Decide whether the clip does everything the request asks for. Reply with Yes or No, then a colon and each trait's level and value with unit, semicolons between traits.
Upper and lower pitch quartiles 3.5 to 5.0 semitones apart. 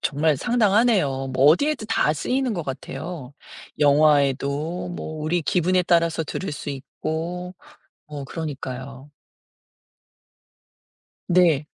Yes: average, 4.1 semitones